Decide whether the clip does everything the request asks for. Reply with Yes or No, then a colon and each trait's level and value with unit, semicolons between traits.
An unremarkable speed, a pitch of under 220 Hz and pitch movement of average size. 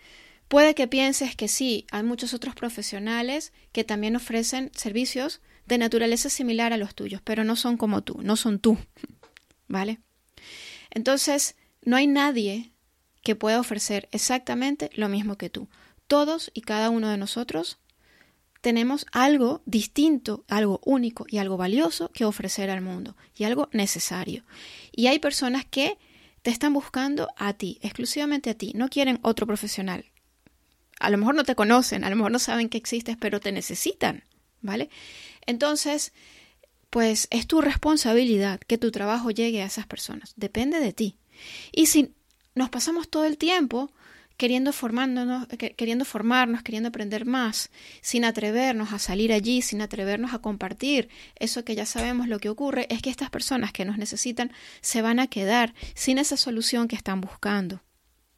No: average, 160 wpm; high, 235 Hz; average, 3.7 semitones